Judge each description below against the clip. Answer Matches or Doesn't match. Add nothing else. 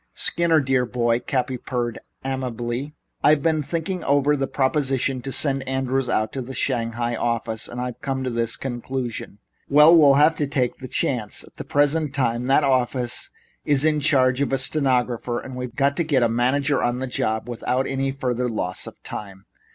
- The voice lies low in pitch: Matches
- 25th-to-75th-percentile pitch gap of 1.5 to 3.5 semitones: Matches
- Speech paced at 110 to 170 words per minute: Doesn't match